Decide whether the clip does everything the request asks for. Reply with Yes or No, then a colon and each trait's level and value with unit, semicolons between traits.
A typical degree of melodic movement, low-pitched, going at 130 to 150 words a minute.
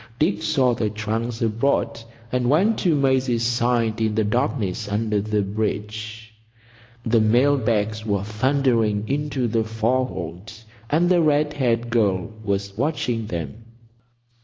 Yes: average, 3.4 semitones; low, 115 Hz; slow, 135 wpm